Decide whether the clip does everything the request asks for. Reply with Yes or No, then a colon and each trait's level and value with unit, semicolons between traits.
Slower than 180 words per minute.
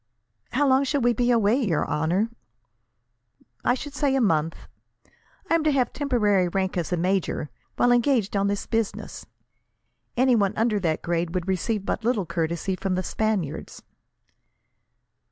Yes: average, 150 wpm